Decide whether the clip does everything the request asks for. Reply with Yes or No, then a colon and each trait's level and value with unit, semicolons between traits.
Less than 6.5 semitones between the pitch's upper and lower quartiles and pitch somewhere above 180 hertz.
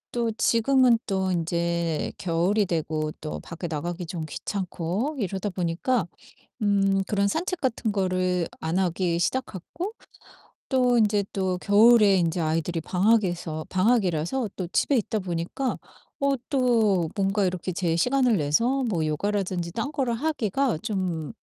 Yes: average, 5.1 semitones; high, 190 Hz